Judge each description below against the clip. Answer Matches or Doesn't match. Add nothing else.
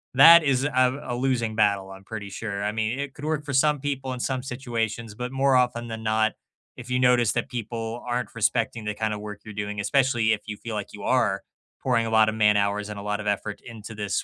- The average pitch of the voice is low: Matches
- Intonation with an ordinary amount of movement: Matches